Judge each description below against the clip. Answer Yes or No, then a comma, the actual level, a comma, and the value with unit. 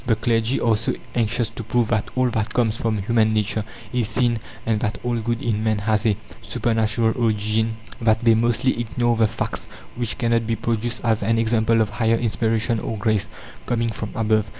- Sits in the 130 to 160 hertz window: No, low, 115 Hz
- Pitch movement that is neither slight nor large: No, narrow, 1.4 semitones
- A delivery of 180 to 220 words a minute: Yes, average, 195 wpm